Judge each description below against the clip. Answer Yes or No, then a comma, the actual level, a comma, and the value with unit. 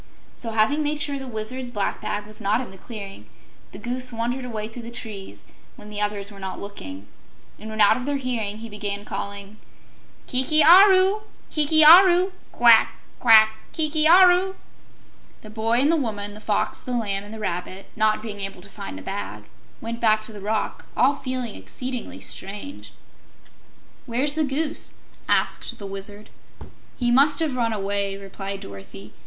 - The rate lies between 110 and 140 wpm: No, average, 170 wpm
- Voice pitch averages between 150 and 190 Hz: No, high, 220 Hz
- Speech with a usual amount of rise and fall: Yes, average, 4.7 semitones